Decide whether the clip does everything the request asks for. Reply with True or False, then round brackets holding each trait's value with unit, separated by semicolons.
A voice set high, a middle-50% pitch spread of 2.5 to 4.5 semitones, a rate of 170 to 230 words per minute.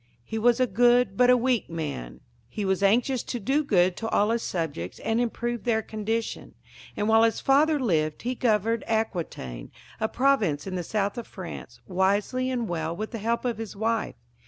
True (220 Hz; 4.1 semitones; 190 wpm)